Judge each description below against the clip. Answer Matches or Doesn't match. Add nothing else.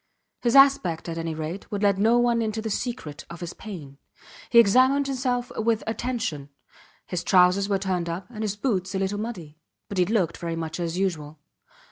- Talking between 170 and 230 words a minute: Matches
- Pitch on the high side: Matches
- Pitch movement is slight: Doesn't match